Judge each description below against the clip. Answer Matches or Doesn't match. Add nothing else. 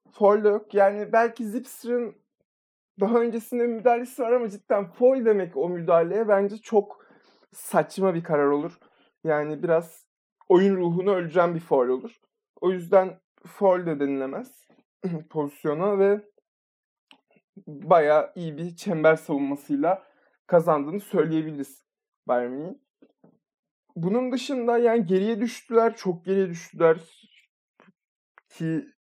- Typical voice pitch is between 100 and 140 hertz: Doesn't match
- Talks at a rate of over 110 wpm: Doesn't match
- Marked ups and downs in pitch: Matches